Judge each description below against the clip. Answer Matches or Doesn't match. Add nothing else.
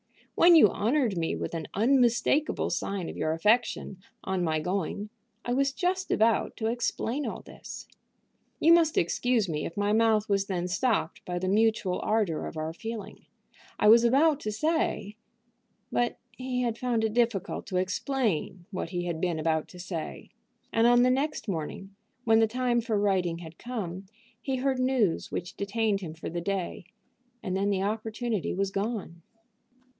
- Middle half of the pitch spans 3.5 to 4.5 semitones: Doesn't match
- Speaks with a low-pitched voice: Doesn't match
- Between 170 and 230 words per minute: Matches